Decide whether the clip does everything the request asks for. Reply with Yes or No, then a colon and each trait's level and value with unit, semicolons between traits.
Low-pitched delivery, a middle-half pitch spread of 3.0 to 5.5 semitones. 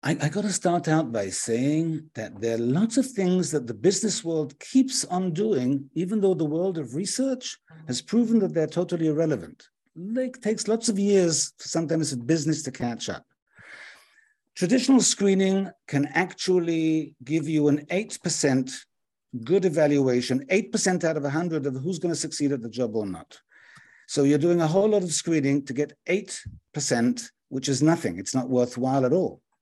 No: medium, 160 Hz; average, 5.2 semitones